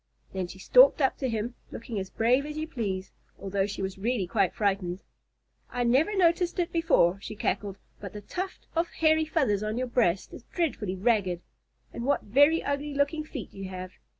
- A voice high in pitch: Yes, high, 230 Hz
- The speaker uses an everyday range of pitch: No, wide, 7.6 semitones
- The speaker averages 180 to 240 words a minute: Yes, average, 190 wpm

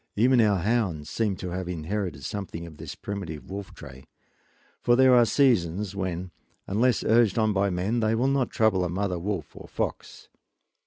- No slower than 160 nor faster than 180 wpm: Yes, average, 175 wpm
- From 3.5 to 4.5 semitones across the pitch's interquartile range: Yes, average, 4.2 semitones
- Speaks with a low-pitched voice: Yes, low, 100 Hz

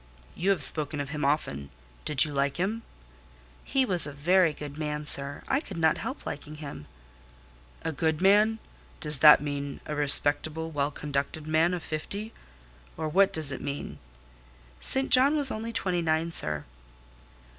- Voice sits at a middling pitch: Yes, medium, 155 Hz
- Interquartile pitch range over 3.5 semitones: Yes, average, 4.1 semitones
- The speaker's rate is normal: Yes, average, 165 wpm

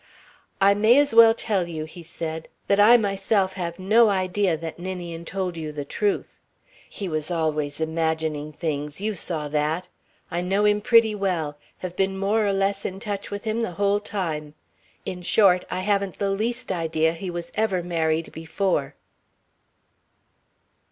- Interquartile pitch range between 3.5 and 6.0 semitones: Yes, average, 3.9 semitones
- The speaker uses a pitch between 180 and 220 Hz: Yes, medium, 185 Hz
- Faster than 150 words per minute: Yes, average, 165 wpm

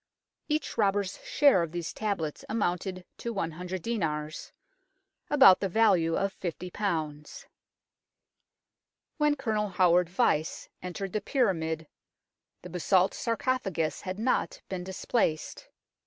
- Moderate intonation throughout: Yes, average, 4.3 semitones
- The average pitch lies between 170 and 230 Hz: Yes, high, 190 Hz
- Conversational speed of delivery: No, slow, 110 wpm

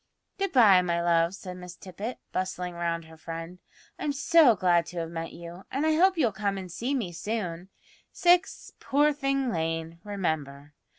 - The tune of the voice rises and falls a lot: Yes, wide, 7.0 semitones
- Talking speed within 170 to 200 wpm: Yes, average, 175 wpm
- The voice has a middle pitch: Yes, medium, 180 Hz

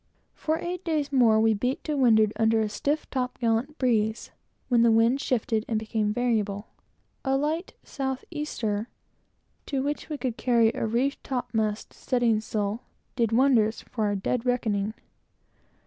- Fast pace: No, average, 155 wpm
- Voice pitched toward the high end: Yes, high, 235 Hz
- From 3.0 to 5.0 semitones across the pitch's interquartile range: Yes, average, 3.5 semitones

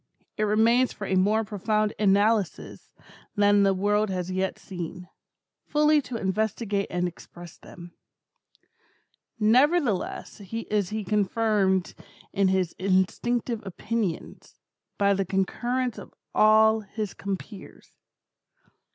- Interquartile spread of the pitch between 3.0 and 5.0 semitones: No, narrow, 2.6 semitones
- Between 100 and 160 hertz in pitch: No, high, 205 Hz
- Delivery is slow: Yes, slow, 110 wpm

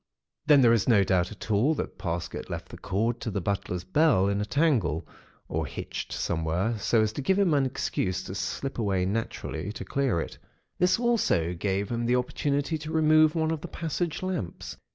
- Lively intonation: Yes, wide, 7.9 semitones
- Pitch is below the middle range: Yes, low, 115 Hz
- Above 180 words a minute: Yes, average, 200 wpm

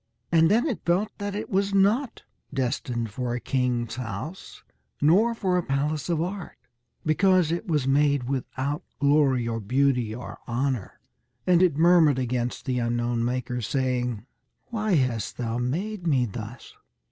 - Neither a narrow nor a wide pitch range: No, wide, 6.2 semitones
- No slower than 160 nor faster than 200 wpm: No, average, 150 wpm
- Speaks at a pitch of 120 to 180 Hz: Yes, medium, 140 Hz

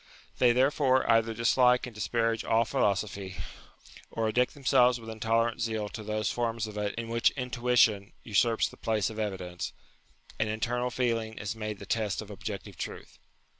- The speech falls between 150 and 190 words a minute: Yes, average, 170 wpm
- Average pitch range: No, narrow, 2.1 semitones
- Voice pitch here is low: Yes, low, 115 Hz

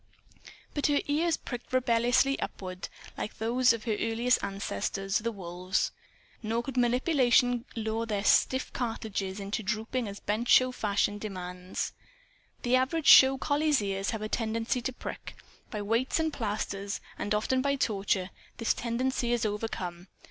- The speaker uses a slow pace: No, average, 150 wpm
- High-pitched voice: Yes, high, 230 Hz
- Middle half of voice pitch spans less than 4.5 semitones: Yes, average, 3.9 semitones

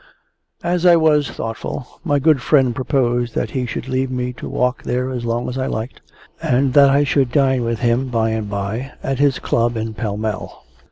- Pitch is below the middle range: Yes, low, 125 Hz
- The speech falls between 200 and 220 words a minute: Yes, fast, 205 wpm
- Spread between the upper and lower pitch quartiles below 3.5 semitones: Yes, average, 2.8 semitones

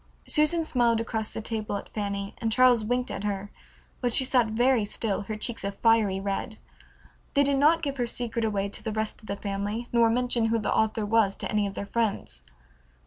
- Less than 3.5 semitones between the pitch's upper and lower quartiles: Yes, average, 2.9 semitones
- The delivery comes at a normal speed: No, fast, 210 wpm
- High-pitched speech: Yes, high, 225 Hz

